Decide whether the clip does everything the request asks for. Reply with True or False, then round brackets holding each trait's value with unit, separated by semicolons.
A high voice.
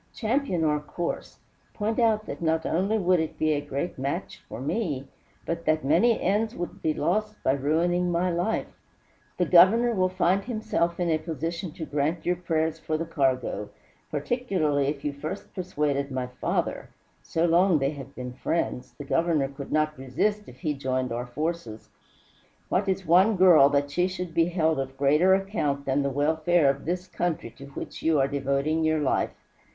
False (160 Hz)